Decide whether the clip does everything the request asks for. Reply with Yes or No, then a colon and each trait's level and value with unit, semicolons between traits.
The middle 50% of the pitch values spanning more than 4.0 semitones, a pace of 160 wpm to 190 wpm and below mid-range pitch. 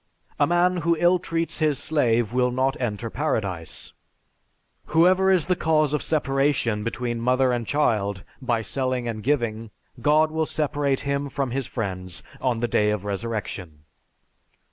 No: average, 5.1 semitones; average, 145 wpm; low, 130 Hz